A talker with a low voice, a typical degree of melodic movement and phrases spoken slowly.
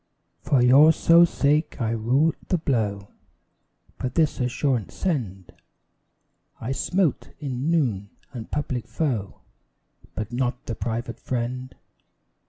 Yes: low, 125 Hz; average, 4.4 semitones; slow, 115 wpm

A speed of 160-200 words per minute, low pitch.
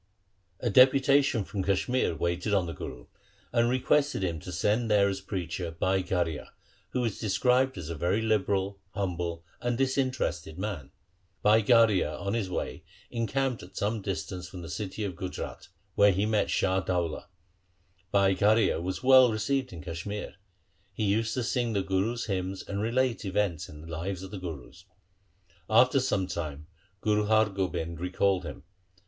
Yes: average, 165 wpm; low, 100 Hz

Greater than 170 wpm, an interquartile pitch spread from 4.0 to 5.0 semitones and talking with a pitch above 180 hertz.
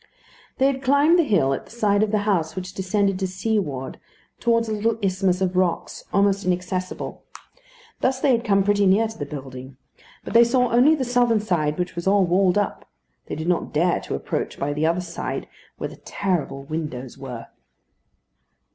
Yes: average, 190 wpm; average, 4.7 semitones; high, 190 Hz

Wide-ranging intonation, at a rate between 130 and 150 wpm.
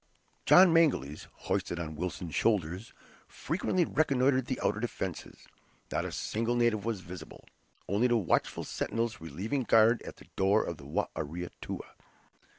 Yes: wide, 5.7 semitones; average, 145 wpm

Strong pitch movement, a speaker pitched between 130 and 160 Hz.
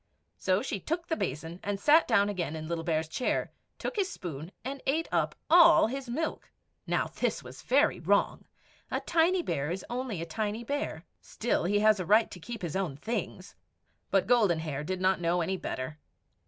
No: wide, 7.2 semitones; high, 200 Hz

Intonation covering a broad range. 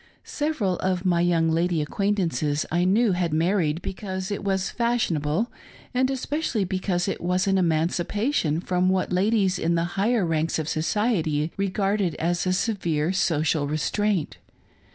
No: average, 3.5 semitones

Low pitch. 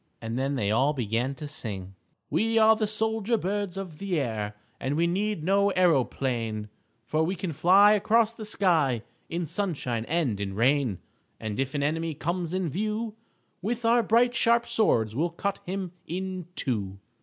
No: medium, 170 Hz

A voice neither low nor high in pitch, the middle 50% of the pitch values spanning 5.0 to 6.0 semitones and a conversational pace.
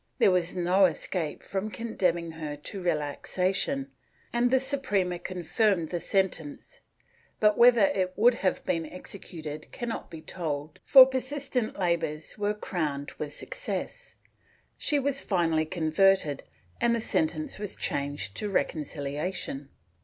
No: medium, 180 Hz; wide, 5.4 semitones; slow, 130 wpm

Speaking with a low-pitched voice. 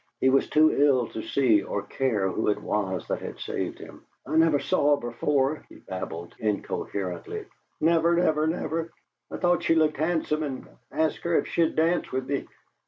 No: medium, 145 Hz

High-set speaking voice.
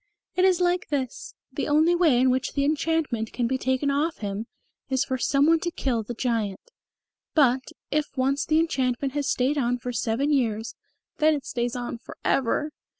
Yes: very high, 265 Hz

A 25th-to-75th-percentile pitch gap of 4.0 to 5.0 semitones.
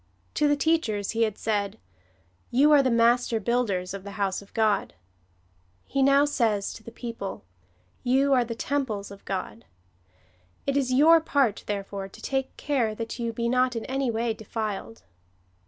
Yes: average, 4.7 semitones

